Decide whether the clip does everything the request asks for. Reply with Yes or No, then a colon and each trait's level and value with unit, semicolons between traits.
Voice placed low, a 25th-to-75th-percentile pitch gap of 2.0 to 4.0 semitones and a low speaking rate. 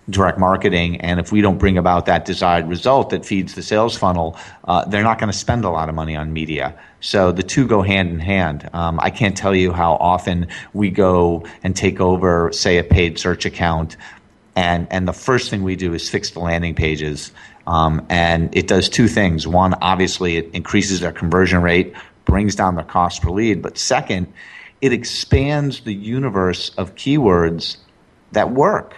No: very low, 90 Hz; average, 2.7 semitones; average, 195 wpm